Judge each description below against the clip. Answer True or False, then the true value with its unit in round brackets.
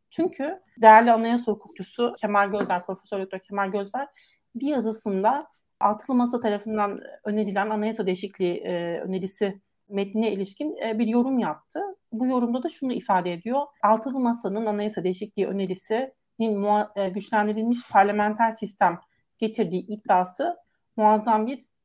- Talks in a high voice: True (215 Hz)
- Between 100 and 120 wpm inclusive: True (115 wpm)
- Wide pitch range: False (3.3 semitones)